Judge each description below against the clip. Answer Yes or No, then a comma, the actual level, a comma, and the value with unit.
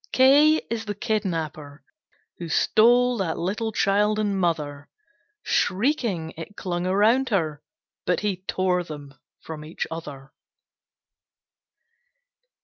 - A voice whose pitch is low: No, medium, 185 Hz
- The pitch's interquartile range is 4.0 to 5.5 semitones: Yes, average, 5.1 semitones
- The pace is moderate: No, slow, 115 wpm